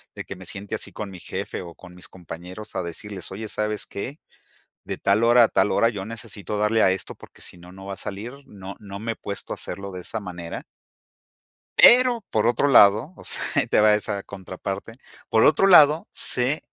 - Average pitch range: Yes, average, 3.1 semitones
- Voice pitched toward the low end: Yes, low, 105 Hz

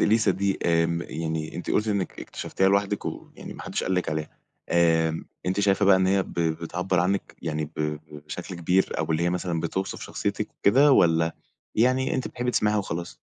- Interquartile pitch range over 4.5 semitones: No, average, 3.4 semitones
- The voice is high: No, very low, 90 Hz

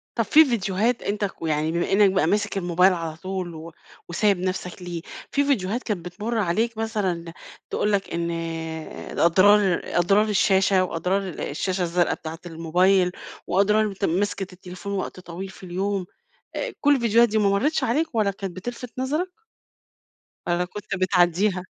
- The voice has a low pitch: No, high, 190 Hz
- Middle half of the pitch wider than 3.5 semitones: No, average, 3.1 semitones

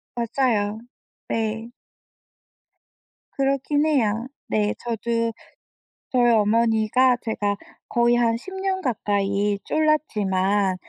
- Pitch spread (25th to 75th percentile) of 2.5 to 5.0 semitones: Yes, average, 3.5 semitones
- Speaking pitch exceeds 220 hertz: Yes, high, 230 Hz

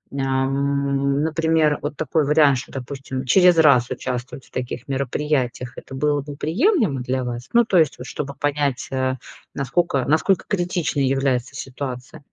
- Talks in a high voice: No, medium, 140 Hz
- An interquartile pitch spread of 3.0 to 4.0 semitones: No, narrow, 2.6 semitones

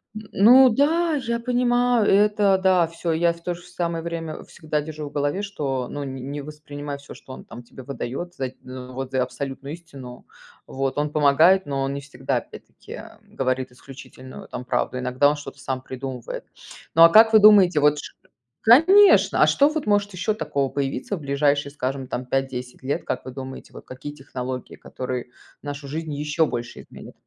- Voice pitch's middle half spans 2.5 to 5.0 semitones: No, wide, 5.4 semitones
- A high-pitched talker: No, medium, 145 Hz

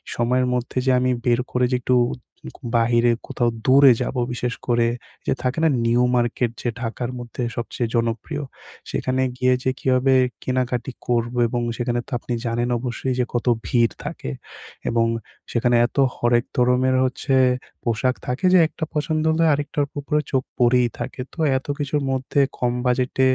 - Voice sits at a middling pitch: No, low, 125 Hz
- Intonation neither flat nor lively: No, narrow, 1.6 semitones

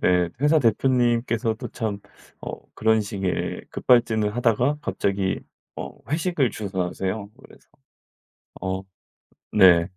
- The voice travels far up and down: No, average, 4.1 semitones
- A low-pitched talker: Yes, low, 110 Hz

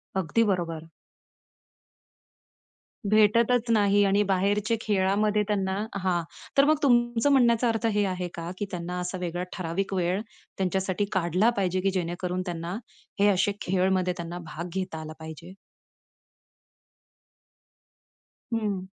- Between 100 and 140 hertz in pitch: No, high, 190 Hz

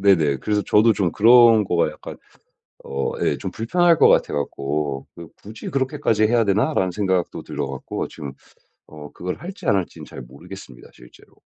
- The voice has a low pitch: Yes, very low, 95 Hz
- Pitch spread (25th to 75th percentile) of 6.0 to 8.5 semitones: Yes, wide, 7.2 semitones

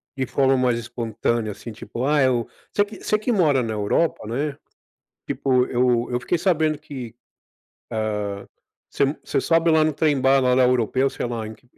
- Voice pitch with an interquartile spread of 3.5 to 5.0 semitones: Yes, average, 4.2 semitones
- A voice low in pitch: Yes, low, 130 Hz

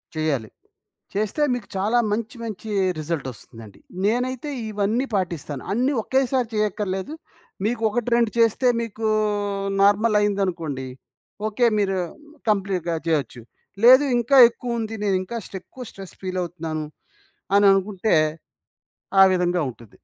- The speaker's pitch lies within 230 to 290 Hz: No, high, 205 Hz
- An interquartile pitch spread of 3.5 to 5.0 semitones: Yes, average, 4.7 semitones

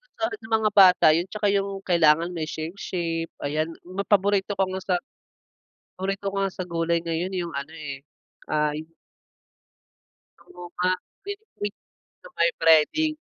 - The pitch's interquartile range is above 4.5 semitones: No, average, 3.3 semitones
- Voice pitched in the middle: Yes, medium, 180 Hz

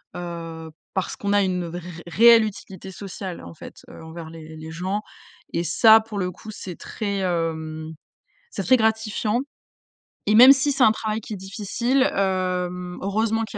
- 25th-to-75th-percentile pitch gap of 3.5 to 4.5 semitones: Yes, average, 4.2 semitones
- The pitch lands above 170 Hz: Yes, high, 190 Hz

